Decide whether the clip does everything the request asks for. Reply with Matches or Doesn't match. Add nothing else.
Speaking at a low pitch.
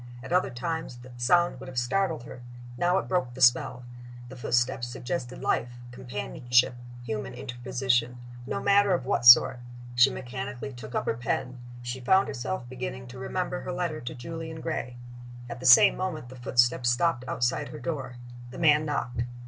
Matches